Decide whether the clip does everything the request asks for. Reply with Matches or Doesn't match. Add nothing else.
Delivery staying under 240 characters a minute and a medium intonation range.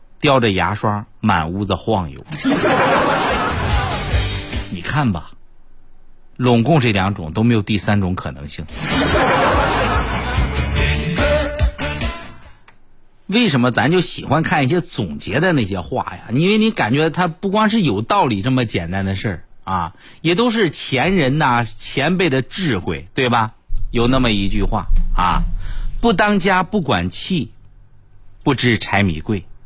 Doesn't match